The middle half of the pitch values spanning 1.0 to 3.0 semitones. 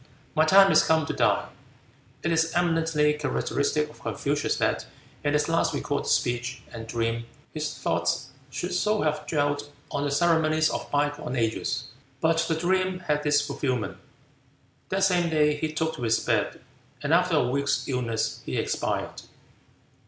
Yes: narrow, 2.6 semitones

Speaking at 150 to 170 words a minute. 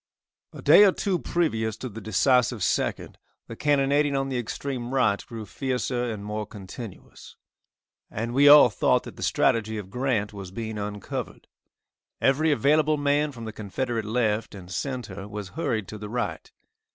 Yes: average, 165 wpm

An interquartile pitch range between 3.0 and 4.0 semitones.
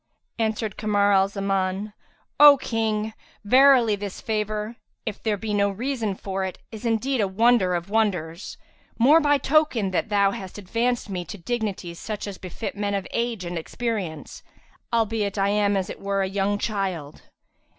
No: narrow, 2.6 semitones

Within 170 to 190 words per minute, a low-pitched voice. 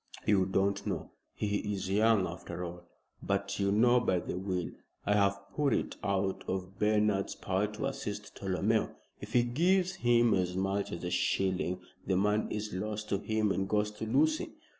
Yes: average, 180 wpm; low, 100 Hz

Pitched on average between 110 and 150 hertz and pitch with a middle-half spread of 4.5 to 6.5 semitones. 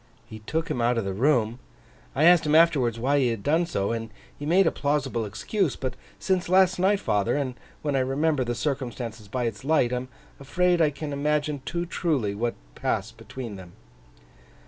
Yes: low, 135 Hz; average, 5.3 semitones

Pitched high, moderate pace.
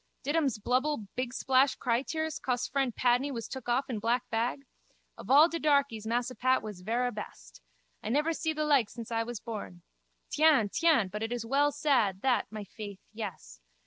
Yes: high, 245 Hz; average, 185 wpm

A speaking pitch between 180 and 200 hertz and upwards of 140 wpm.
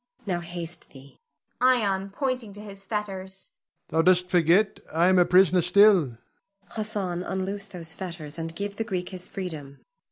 Yes: medium, 185 Hz; average, 160 wpm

